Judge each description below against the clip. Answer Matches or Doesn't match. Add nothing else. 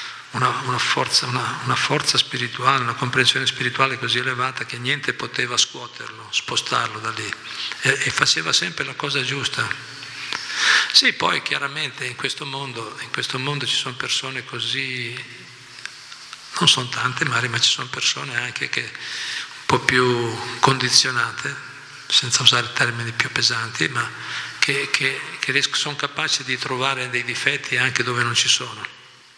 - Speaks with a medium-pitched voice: Doesn't match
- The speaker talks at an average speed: Matches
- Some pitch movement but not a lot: Doesn't match